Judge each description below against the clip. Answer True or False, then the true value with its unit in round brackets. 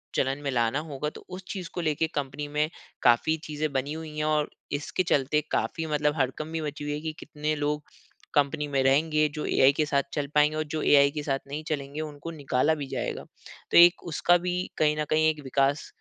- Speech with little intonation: True (1.7 semitones)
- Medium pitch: True (150 Hz)